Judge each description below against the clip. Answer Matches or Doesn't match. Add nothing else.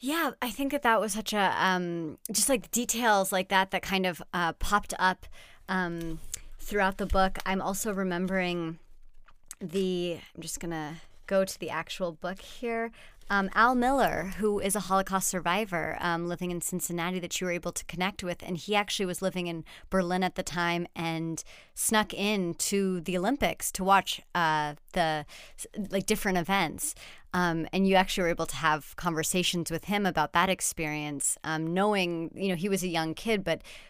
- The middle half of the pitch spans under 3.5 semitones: Matches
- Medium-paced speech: Matches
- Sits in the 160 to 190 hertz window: Matches